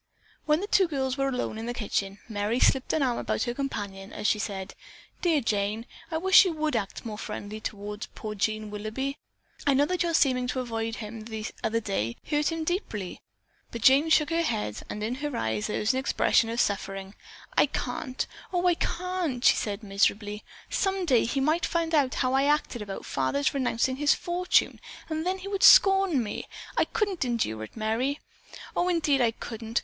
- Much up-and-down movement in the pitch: Yes, wide, 6.6 semitones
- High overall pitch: Yes, very high, 250 Hz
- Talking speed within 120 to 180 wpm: No, average, 200 wpm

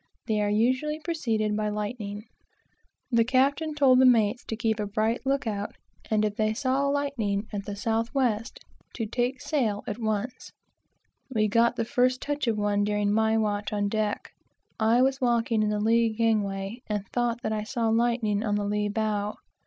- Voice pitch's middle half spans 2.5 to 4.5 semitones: Yes, average, 2.9 semitones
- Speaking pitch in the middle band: No, high, 220 Hz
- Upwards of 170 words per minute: Yes, average, 185 wpm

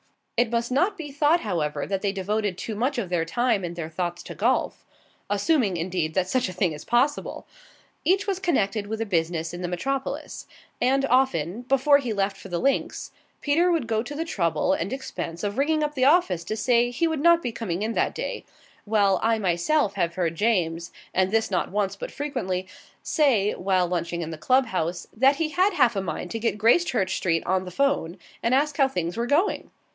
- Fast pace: Yes, fast, 210 wpm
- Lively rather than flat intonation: Yes, wide, 7.1 semitones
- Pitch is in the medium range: No, high, 215 Hz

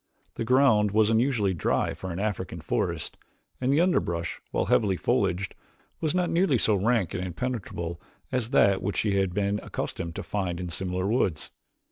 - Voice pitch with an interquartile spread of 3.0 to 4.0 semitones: No, average, 4.8 semitones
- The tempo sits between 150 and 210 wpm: Yes, average, 170 wpm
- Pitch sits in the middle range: No, low, 100 Hz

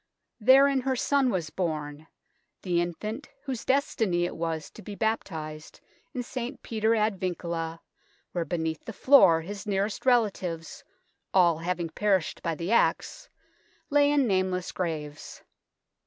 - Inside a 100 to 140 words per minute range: Yes, slow, 135 wpm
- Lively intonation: Yes, wide, 5.9 semitones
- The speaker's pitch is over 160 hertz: Yes, medium, 185 Hz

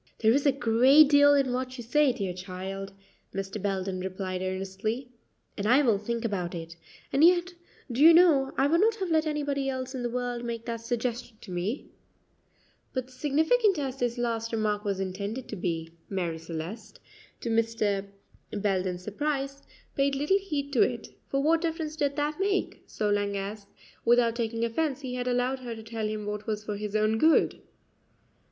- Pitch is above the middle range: Yes, high, 235 Hz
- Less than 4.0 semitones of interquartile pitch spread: No, average, 5.3 semitones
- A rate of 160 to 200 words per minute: Yes, average, 185 wpm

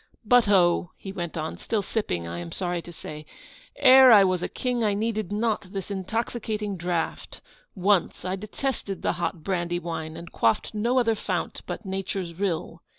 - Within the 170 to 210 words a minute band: Yes, average, 175 wpm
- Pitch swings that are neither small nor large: Yes, average, 3.9 semitones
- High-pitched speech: Yes, high, 195 Hz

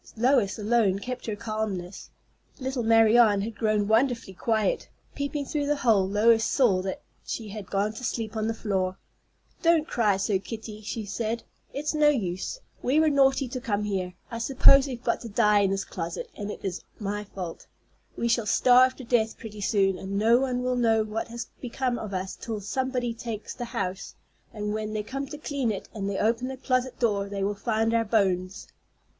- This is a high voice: Yes, high, 220 Hz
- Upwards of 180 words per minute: Yes, average, 195 wpm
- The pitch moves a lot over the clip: No, average, 3.5 semitones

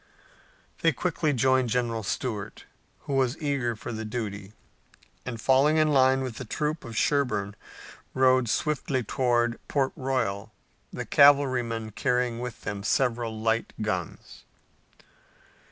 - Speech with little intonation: No, average, 3.1 semitones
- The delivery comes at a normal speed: No, slow, 125 wpm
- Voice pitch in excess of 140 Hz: No, low, 125 Hz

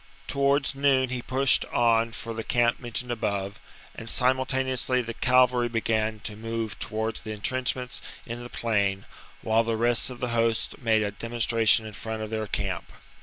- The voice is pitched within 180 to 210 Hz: No, low, 115 Hz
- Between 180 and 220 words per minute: No, average, 170 wpm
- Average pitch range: No, narrow, 2.3 semitones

